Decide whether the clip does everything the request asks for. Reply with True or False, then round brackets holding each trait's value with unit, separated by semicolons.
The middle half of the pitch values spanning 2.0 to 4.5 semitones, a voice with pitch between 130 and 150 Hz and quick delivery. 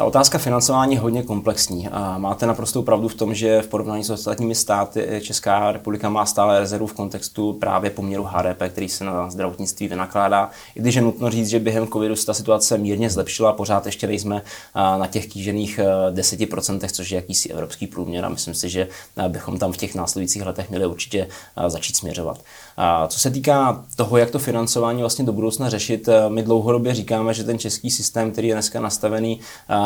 False (2.5 semitones; 105 Hz; 185 wpm)